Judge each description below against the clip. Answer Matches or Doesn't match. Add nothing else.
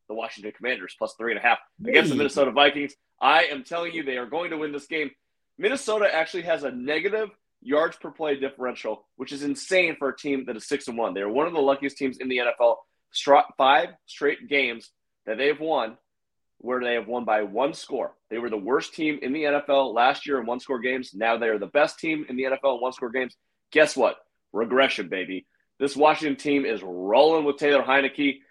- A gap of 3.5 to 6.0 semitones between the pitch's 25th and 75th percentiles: Doesn't match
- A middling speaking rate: Doesn't match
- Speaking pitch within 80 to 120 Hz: Doesn't match